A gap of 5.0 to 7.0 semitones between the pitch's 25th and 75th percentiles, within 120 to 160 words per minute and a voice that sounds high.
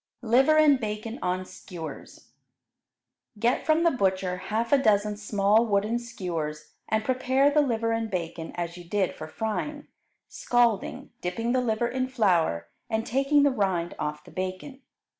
Yes: wide, 5.4 semitones; average, 155 wpm; high, 220 Hz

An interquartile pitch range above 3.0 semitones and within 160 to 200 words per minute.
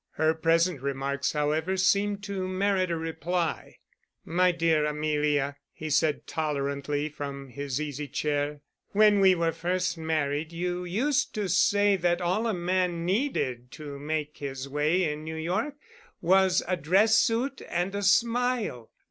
No: average, 4.1 semitones; average, 150 wpm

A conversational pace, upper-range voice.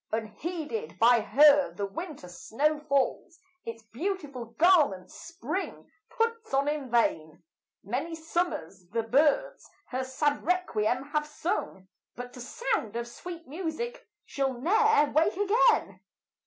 No: slow, 125 wpm; very high, 290 Hz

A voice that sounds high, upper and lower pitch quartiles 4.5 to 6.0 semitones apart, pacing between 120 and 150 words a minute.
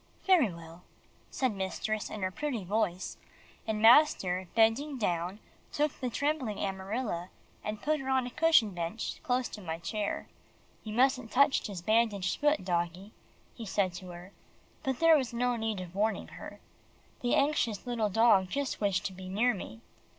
No: high, 215 Hz; average, 5.2 semitones; average, 165 wpm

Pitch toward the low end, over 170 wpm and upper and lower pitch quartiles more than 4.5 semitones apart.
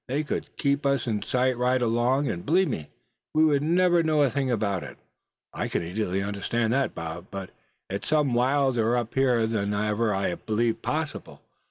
Yes: low, 120 Hz; average, 185 wpm; average, 5.1 semitones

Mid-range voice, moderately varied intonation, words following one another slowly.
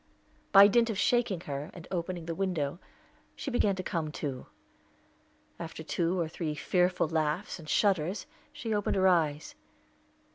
No: medium, 175 Hz; average, 3.6 semitones; average, 150 wpm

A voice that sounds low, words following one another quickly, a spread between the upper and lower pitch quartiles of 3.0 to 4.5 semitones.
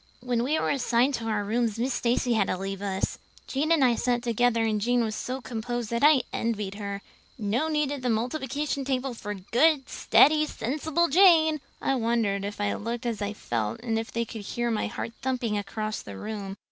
No: high, 235 Hz; fast, 210 wpm; average, 3.9 semitones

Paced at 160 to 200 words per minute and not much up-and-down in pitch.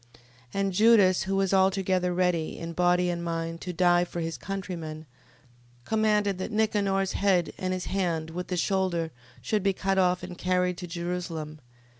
Yes: average, 170 wpm; narrow, 2.1 semitones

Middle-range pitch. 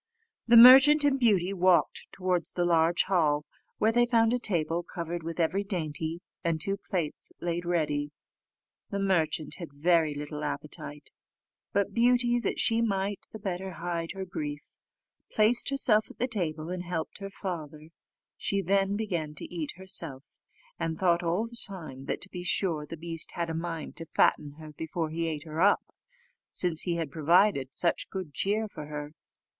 Yes: medium, 175 Hz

